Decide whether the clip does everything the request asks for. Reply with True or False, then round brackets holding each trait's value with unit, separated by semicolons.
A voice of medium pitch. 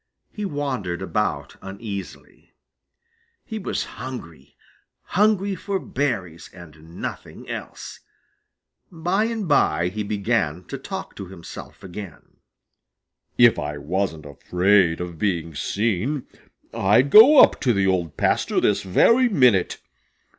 False (100 Hz)